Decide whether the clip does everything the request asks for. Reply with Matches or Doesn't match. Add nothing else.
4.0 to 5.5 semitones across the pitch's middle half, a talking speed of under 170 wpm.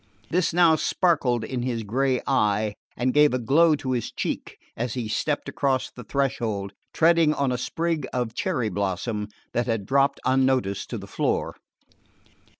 Matches